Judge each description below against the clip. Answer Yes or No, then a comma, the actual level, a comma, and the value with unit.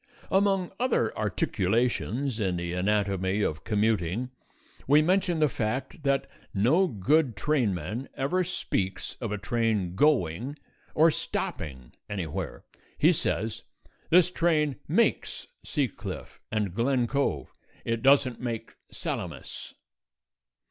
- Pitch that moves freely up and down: Yes, wide, 6.6 semitones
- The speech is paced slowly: Yes, slow, 115 wpm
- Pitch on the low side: Yes, low, 115 Hz